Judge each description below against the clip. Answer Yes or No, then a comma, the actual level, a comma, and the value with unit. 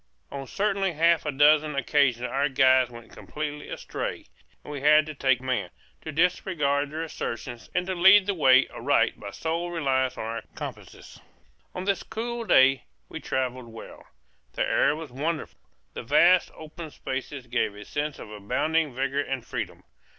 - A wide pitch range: No, average, 3.9 semitones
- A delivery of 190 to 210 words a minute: No, average, 165 wpm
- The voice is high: No, medium, 145 Hz